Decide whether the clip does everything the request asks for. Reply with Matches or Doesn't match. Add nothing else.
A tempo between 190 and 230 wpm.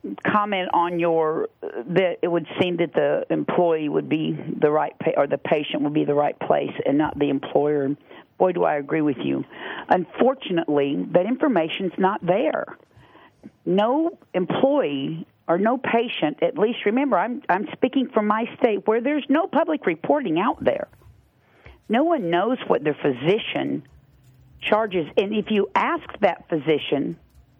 Doesn't match